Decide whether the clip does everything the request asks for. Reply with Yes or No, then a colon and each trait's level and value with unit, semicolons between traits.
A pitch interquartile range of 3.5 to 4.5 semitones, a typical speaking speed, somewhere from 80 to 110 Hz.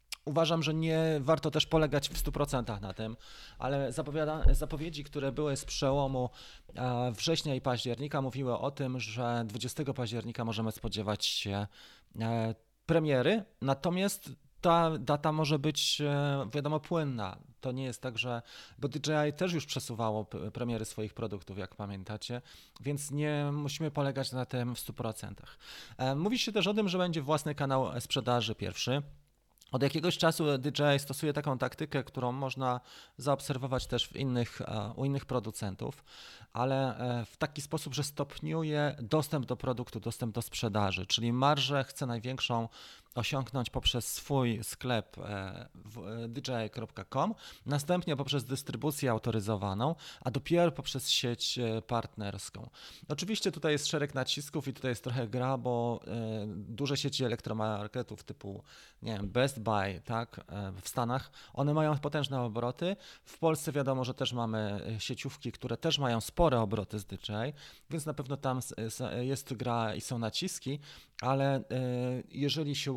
No: average, 4.0 semitones; average, 140 wpm; low, 130 Hz